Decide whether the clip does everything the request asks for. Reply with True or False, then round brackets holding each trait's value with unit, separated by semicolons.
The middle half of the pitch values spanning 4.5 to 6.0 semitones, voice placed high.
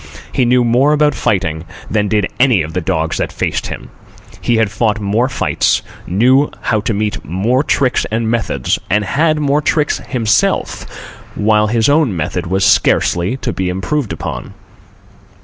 False (5.2 semitones; 110 Hz)